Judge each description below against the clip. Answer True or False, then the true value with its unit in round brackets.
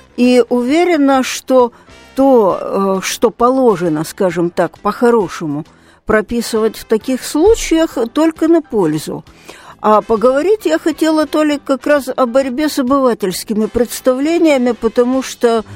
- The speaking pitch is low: False (250 Hz)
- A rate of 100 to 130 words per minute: True (115 wpm)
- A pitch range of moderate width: True (4.9 semitones)